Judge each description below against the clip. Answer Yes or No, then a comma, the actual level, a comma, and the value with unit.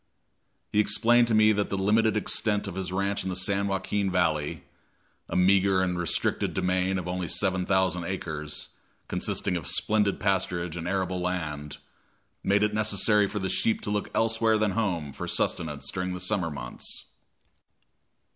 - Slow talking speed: No, average, 165 wpm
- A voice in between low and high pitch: No, very low, 95 Hz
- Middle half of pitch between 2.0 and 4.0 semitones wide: Yes, narrow, 2.6 semitones